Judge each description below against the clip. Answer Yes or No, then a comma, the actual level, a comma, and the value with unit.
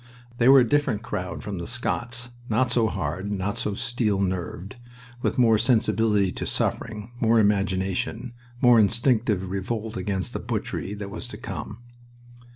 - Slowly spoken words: No, average, 155 wpm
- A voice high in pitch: No, low, 105 Hz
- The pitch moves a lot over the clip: No, average, 3.3 semitones